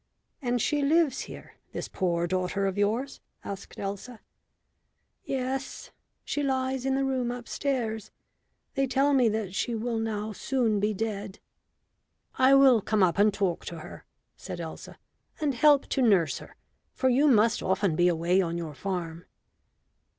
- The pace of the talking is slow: No, average, 155 wpm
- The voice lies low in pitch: No, high, 220 Hz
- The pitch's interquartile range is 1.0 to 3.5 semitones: No, wide, 5.4 semitones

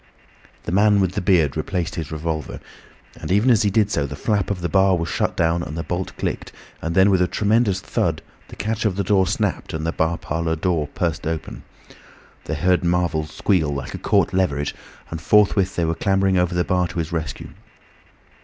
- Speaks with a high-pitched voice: No, very low, 90 Hz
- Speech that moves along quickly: Yes, fast, 210 wpm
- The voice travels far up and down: No, average, 3.1 semitones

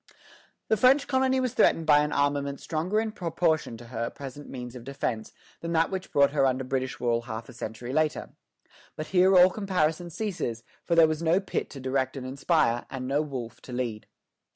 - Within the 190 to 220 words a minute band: Yes, average, 200 wpm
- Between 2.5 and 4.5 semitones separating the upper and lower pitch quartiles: No, average, 5.3 semitones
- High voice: No, medium, 145 Hz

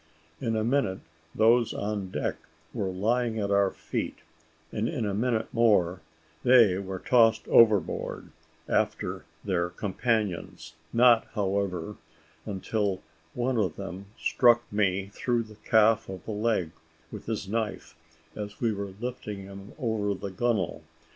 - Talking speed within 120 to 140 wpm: Yes, slow, 135 wpm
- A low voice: Yes, low, 105 Hz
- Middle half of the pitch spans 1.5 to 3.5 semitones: Yes, average, 3.0 semitones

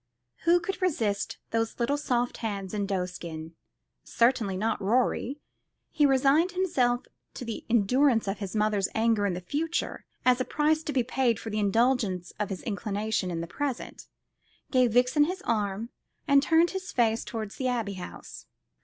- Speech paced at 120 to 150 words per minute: No, average, 165 wpm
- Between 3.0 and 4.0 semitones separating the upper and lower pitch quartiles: No, average, 5.1 semitones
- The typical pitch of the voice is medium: No, high, 230 Hz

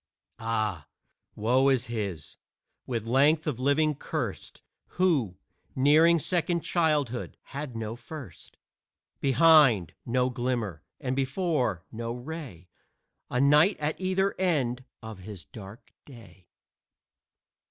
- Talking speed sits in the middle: No, slow, 110 wpm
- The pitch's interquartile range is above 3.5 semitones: Yes, average, 5.3 semitones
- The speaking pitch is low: Yes, low, 130 Hz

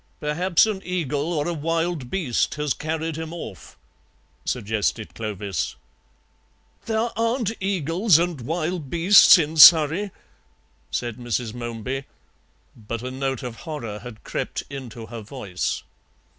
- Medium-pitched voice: Yes, medium, 150 Hz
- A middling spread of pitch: No, wide, 6.4 semitones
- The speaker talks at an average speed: No, slow, 125 wpm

